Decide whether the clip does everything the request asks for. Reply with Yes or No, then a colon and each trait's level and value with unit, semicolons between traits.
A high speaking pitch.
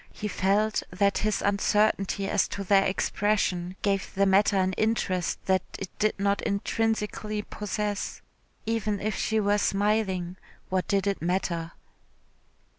Yes: high, 200 Hz